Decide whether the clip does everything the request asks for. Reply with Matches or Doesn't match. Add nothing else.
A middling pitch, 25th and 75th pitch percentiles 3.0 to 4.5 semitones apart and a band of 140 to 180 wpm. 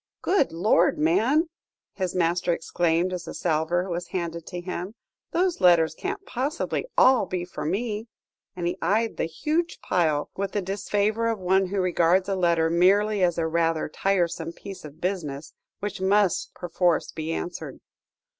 Matches